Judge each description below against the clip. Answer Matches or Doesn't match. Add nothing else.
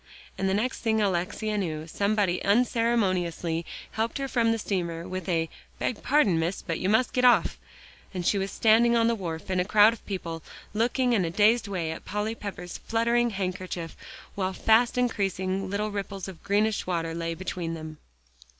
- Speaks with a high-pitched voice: Matches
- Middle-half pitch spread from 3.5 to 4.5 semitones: Matches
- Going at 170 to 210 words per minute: Matches